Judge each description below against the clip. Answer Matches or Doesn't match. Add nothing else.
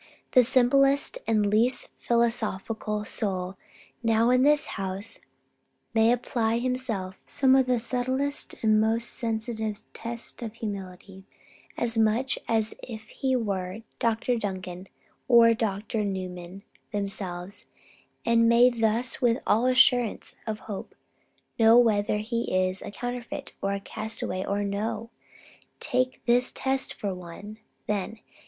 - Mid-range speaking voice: Doesn't match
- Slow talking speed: Matches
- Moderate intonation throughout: Matches